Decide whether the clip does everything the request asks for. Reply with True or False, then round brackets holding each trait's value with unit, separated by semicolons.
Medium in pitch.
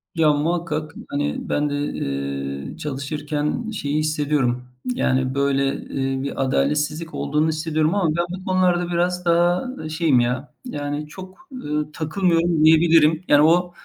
True (155 Hz)